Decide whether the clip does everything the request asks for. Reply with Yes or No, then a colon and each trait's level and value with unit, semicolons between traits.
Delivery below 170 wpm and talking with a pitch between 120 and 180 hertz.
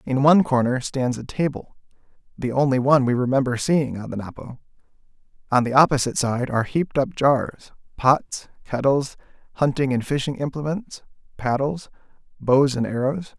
Yes: average, 150 wpm; low, 135 Hz